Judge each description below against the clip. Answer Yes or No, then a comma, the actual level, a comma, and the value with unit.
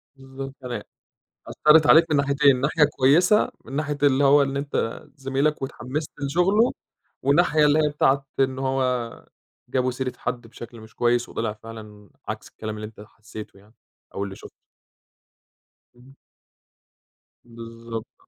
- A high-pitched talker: No, low, 135 Hz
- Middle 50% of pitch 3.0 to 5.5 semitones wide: Yes, average, 3.8 semitones